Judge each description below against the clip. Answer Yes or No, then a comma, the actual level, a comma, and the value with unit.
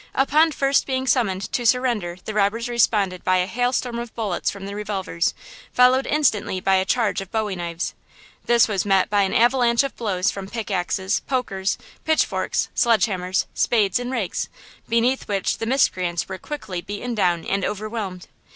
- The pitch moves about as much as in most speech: Yes, average, 4.3 semitones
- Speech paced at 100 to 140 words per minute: No, average, 180 wpm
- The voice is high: Yes, high, 210 Hz